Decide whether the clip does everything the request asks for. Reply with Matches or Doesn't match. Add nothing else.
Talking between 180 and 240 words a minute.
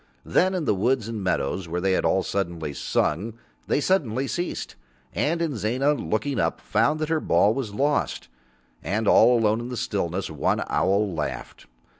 Doesn't match